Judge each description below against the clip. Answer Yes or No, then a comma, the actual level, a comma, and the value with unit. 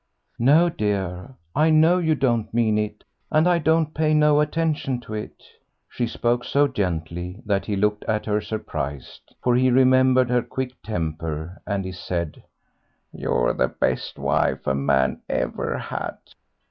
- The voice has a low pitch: Yes, low, 115 Hz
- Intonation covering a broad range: Yes, wide, 7.7 semitones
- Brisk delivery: No, average, 155 wpm